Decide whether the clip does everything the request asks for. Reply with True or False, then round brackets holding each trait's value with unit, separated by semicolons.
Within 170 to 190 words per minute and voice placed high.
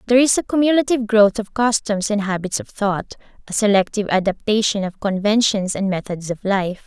True (175 wpm; 210 Hz)